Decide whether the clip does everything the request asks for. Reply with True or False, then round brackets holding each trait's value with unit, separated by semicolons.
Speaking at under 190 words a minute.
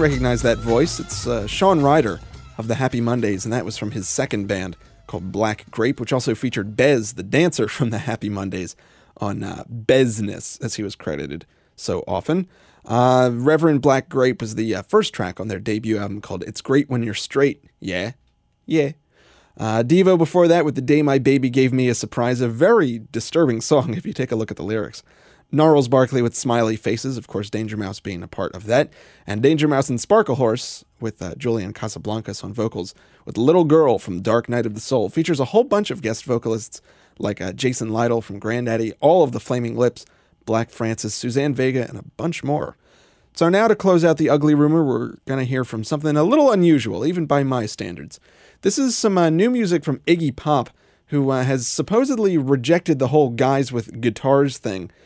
False (205 wpm)